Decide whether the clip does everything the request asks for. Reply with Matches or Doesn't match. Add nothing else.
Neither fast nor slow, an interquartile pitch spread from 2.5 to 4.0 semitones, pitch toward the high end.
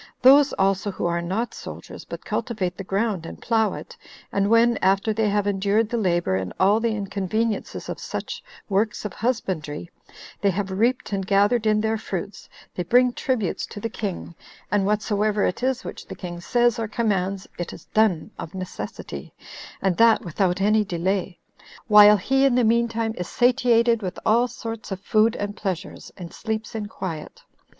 Matches